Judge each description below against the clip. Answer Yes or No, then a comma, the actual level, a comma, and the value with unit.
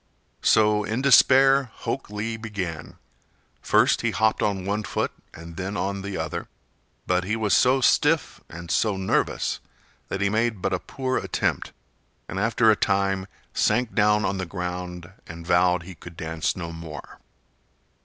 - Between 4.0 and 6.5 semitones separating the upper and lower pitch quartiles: No, average, 3.6 semitones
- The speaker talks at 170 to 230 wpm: No, average, 160 wpm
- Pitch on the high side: No, low, 100 Hz